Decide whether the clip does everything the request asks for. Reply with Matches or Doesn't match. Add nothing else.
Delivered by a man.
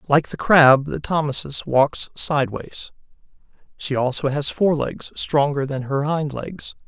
Matches